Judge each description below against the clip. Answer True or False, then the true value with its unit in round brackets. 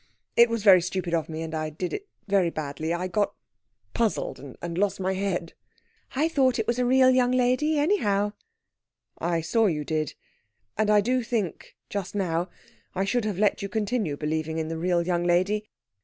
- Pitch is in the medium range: False (195 Hz)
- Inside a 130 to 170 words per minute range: False (185 wpm)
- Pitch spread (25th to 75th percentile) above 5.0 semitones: True (5.4 semitones)